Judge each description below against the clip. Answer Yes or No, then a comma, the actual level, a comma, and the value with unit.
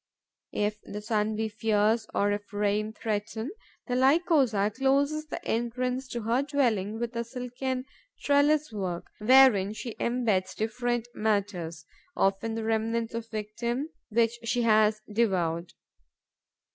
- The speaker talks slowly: Yes, slow, 130 wpm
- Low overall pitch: No, high, 225 Hz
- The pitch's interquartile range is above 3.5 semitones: No, average, 3.0 semitones